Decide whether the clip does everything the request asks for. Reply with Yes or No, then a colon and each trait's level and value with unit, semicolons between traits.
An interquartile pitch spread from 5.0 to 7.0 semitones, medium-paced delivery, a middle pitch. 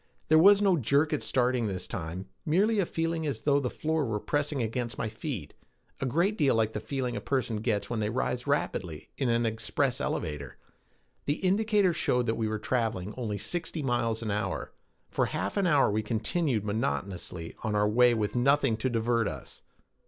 No: wide, 5.4 semitones; average, 190 wpm; low, 120 Hz